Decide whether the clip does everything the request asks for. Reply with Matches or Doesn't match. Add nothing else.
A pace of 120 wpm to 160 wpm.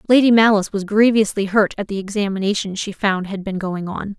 Doesn't match